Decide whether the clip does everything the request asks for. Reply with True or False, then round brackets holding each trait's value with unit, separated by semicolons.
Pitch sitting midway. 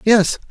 False (210 Hz)